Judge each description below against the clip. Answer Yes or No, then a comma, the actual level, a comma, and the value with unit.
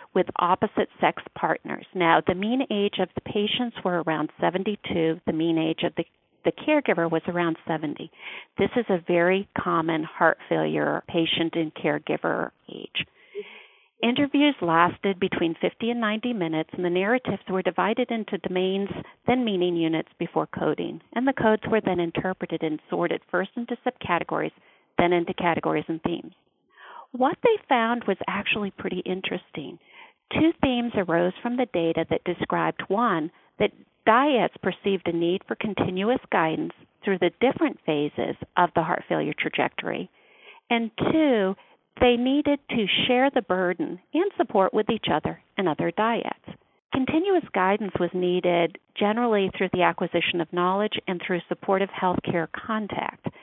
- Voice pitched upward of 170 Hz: Yes, high, 190 Hz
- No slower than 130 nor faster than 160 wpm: Yes, average, 150 wpm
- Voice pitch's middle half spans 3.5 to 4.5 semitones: No, wide, 5.6 semitones